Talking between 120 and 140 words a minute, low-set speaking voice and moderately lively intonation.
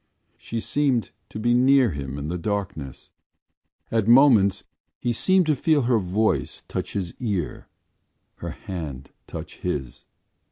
No: slow, 135 wpm; low, 105 Hz; wide, 6.5 semitones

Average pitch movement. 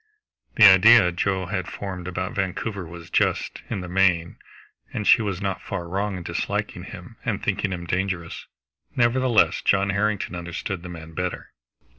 No: narrow, 2.3 semitones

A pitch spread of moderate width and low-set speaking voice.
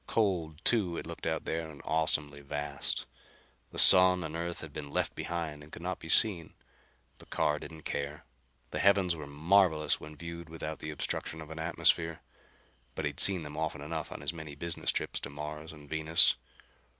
No: narrow, 2.2 semitones; very low, 80 Hz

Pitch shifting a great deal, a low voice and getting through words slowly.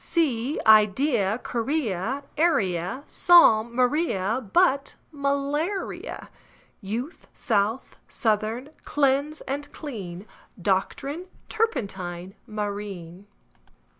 No: wide, 6.1 semitones; high, 240 Hz; slow, 75 wpm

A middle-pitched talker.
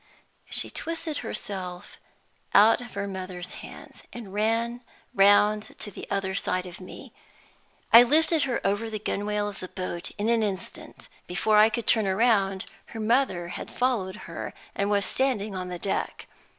No: high, 205 Hz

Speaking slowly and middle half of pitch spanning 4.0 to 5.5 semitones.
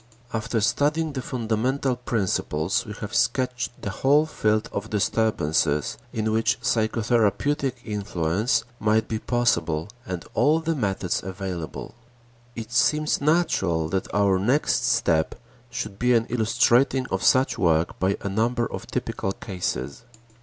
Yes: slow, 130 wpm; average, 4.4 semitones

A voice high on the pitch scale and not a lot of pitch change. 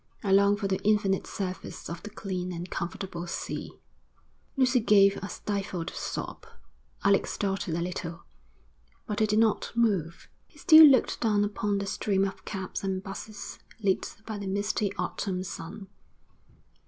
Yes: high, 200 Hz; narrow, 1.9 semitones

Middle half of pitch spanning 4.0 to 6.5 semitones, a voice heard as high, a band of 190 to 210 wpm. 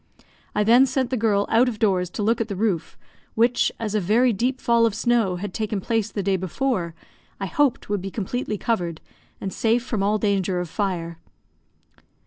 No: average, 3.5 semitones; high, 215 Hz; average, 195 wpm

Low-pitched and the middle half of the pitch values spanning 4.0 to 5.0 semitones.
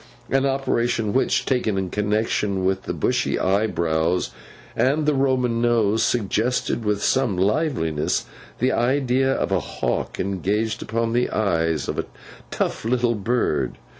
Yes: low, 110 Hz; average, 4.4 semitones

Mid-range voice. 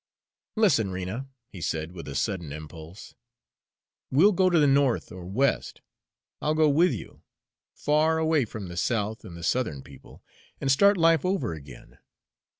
No: low, 115 Hz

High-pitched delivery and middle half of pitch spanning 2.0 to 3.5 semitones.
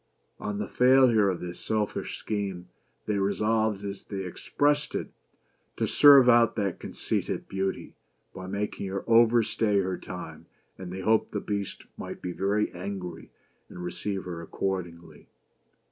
No: low, 100 Hz; average, 2.8 semitones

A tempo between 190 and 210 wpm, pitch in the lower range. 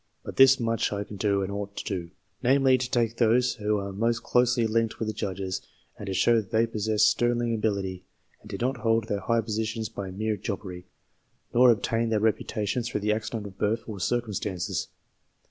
Yes: average, 200 wpm; low, 110 Hz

